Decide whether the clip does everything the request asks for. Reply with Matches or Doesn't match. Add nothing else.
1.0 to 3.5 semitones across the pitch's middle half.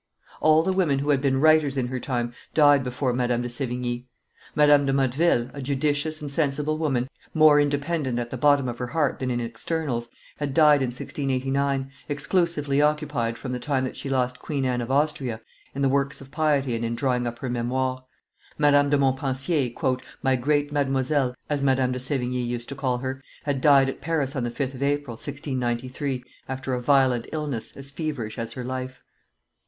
Matches